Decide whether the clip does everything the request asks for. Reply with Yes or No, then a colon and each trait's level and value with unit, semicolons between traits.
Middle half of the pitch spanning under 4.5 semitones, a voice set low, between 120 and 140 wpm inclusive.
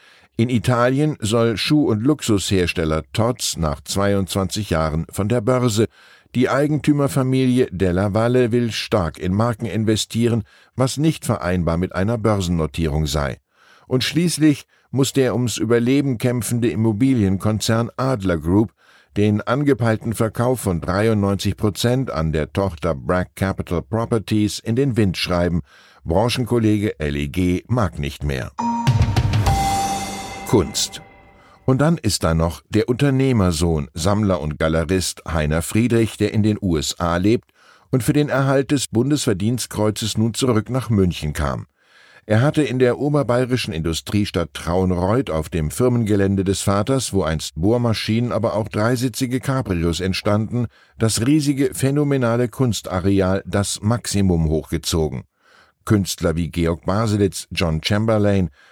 No: average, 5.3 semitones; low, 105 Hz; slow, 125 wpm